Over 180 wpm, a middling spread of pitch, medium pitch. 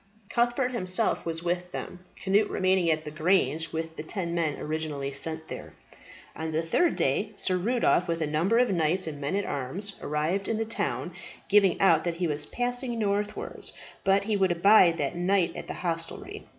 Yes: average, 190 wpm; average, 4.0 semitones; medium, 180 Hz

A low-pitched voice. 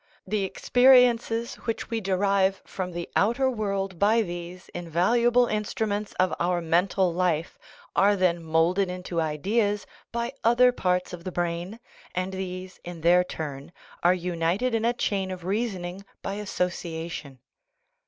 No: medium, 185 Hz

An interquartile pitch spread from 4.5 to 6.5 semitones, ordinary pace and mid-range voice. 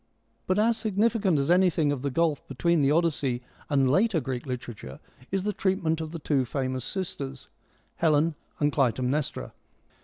Yes: wide, 5.5 semitones; average, 160 wpm; medium, 150 Hz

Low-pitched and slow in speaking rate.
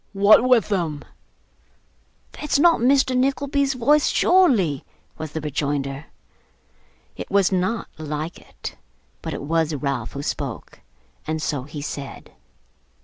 No: medium, 165 Hz; slow, 125 wpm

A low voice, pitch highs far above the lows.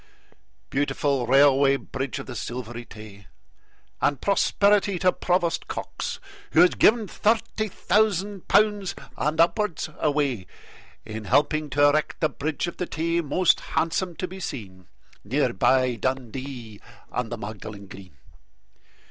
No: medium, 145 Hz; wide, 6.7 semitones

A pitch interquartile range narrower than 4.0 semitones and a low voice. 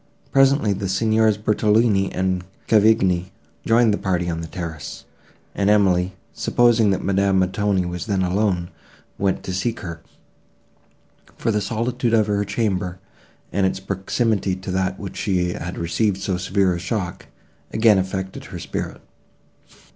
Yes: average, 2.8 semitones; very low, 95 Hz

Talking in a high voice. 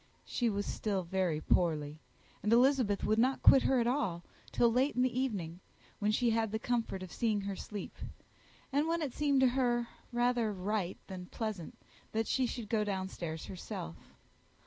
Yes: high, 220 Hz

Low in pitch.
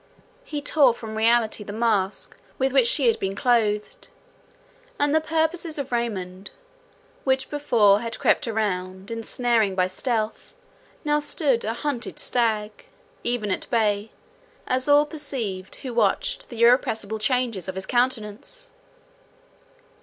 No: high, 235 Hz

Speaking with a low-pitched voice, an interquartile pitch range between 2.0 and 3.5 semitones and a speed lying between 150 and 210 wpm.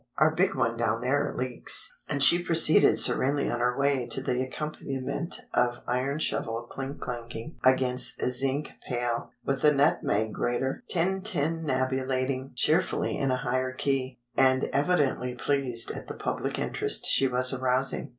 No: low, 130 Hz; narrow, 2.4 semitones; average, 140 wpm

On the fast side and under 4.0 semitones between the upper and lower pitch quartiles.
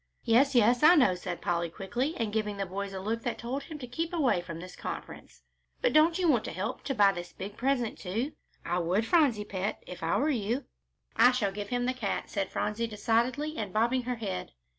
No: fast, 225 wpm; average, 4.8 semitones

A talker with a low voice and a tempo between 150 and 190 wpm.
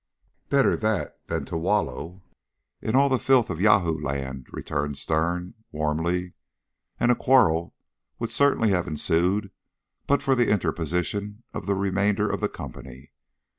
No: very low, 90 Hz; average, 140 wpm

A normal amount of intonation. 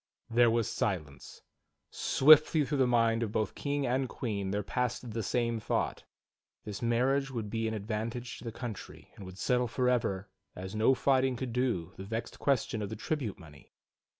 Yes: average, 3.2 semitones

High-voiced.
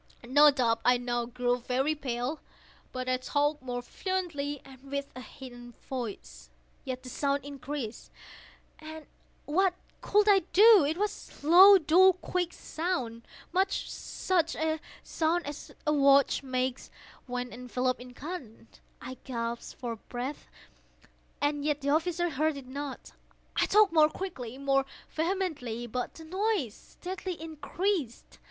Yes: very high, 280 Hz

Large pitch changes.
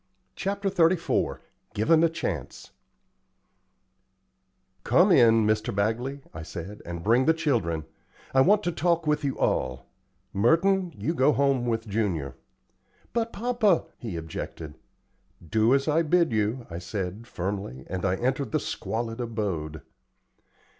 Yes: wide, 9.0 semitones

